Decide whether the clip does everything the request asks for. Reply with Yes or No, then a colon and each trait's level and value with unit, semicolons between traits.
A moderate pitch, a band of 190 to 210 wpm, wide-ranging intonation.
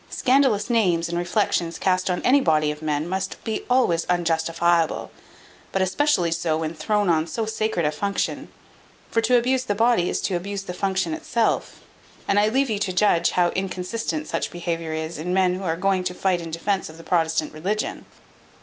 No: medium, 180 Hz; average, 195 wpm; average, 4.1 semitones